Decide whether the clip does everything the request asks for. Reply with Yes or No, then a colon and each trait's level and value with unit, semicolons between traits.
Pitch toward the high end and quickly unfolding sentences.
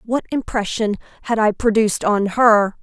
No: high, 220 Hz; average, 150 wpm